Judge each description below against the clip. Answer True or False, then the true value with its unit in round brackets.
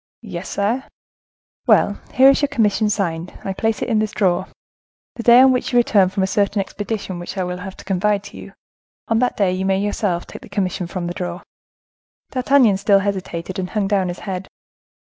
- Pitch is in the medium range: False (200 Hz)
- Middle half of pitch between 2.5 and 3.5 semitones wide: True (2.8 semitones)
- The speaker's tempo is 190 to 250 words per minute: True (205 wpm)